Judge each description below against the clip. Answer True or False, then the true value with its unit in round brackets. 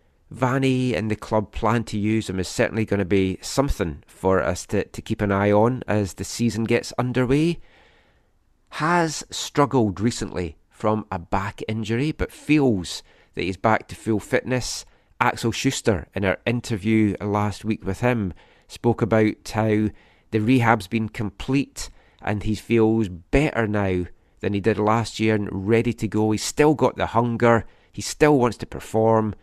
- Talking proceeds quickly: False (165 wpm)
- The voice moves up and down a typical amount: True (3.0 semitones)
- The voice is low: True (110 Hz)